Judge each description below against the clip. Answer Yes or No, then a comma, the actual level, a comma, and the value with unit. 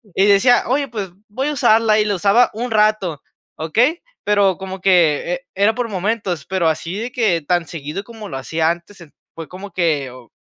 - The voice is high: Yes, high, 195 Hz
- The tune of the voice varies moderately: Yes, average, 4.5 semitones